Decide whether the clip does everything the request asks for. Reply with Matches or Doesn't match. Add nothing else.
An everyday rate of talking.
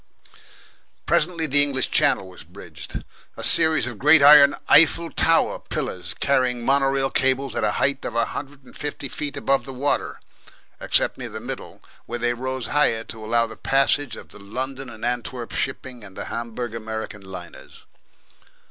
Matches